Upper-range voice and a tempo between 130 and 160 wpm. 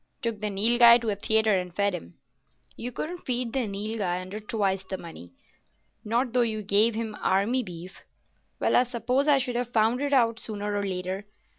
No: high, 215 Hz; average, 185 wpm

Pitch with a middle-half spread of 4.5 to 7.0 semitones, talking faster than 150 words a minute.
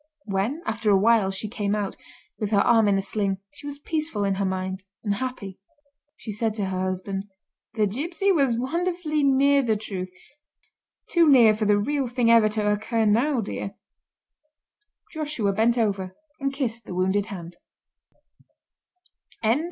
Yes: average, 4.9 semitones; average, 160 wpm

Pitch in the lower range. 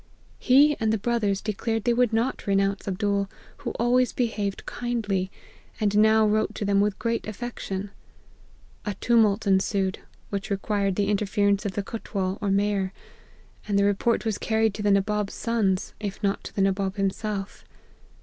No: high, 205 Hz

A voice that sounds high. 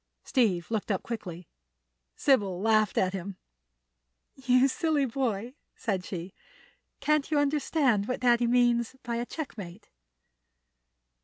Yes: high, 235 Hz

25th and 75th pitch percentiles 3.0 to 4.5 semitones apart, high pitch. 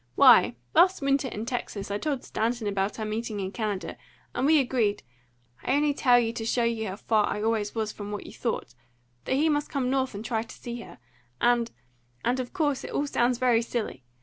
Yes: average, 3.4 semitones; high, 235 Hz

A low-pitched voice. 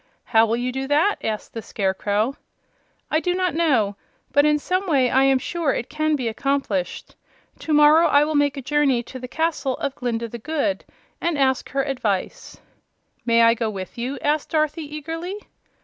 No: very high, 275 Hz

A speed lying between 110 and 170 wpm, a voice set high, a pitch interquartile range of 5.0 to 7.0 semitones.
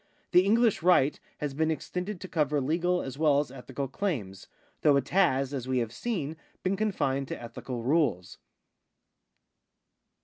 No: average, 150 wpm; medium, 150 Hz; average, 5.3 semitones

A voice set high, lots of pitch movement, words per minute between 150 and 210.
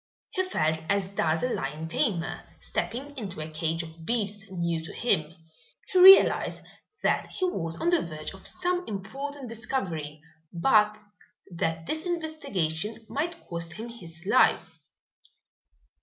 No: high, 195 Hz; wide, 8.7 semitones; average, 140 wpm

